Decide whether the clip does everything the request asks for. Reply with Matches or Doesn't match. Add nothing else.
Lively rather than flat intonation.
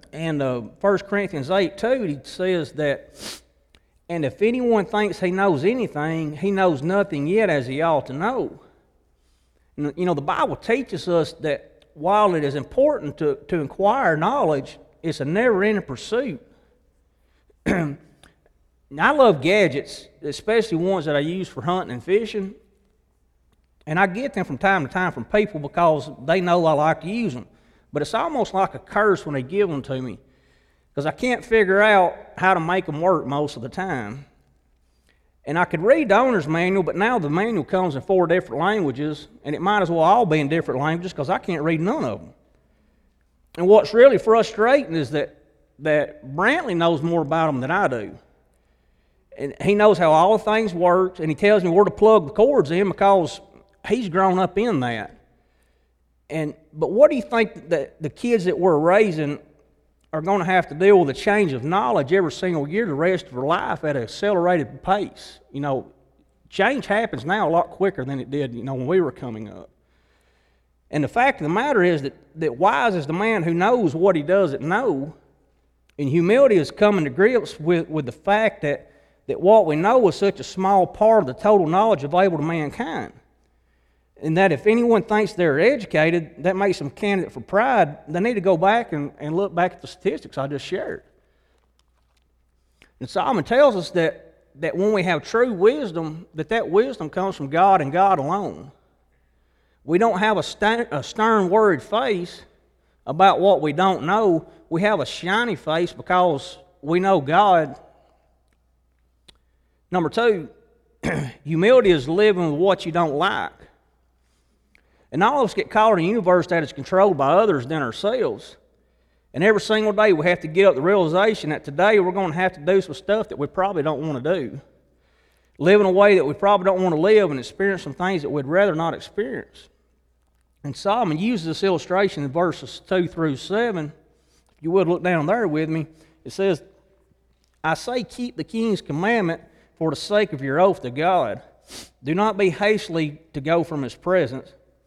Matches